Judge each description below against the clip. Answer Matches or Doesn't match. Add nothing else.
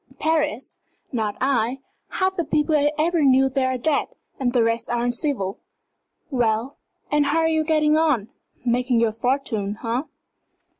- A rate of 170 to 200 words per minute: Doesn't match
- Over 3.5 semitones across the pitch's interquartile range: Matches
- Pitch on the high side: Matches